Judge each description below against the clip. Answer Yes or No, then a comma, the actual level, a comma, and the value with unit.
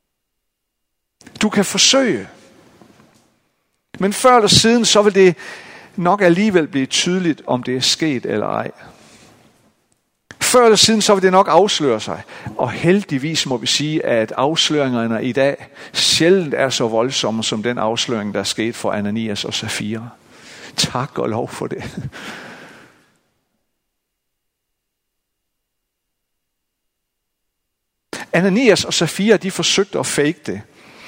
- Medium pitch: Yes, medium, 150 Hz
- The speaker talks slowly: Yes, slow, 125 wpm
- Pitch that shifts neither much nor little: No, wide, 8.6 semitones